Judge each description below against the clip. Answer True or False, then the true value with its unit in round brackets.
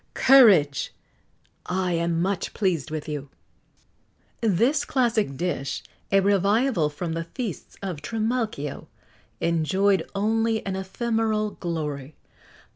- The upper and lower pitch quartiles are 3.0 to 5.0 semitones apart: False (5.4 semitones)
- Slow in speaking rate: True (105 wpm)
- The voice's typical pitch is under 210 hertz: True (190 Hz)